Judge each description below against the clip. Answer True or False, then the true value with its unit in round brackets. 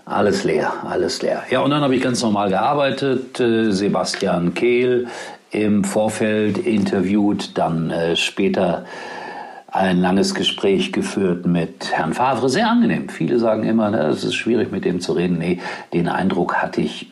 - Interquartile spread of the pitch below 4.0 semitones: False (4.6 semitones)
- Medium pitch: False (110 Hz)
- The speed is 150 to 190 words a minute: True (155 wpm)